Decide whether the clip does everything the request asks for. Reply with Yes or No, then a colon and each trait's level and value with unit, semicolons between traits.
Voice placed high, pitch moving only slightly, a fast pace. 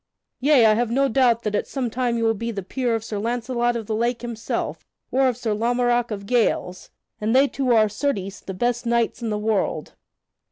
Yes: high, 235 Hz; narrow, 2.2 semitones; fast, 215 wpm